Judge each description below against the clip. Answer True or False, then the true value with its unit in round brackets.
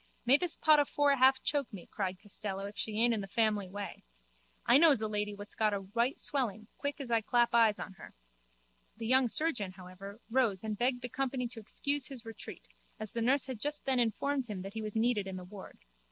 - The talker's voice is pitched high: True (225 Hz)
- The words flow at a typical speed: False (225 wpm)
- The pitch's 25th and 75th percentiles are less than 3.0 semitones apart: False (4.3 semitones)